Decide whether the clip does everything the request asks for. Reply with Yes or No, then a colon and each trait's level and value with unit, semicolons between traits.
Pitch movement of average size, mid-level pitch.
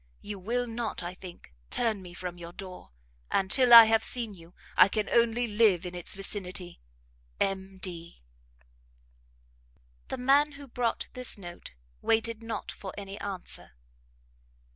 No: average, 4.2 semitones; high, 200 Hz